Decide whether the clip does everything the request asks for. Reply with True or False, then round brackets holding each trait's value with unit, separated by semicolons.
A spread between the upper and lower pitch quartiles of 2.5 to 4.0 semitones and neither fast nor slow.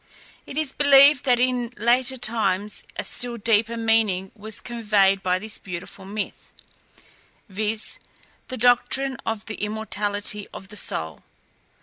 False (3.2 semitones; 130 wpm)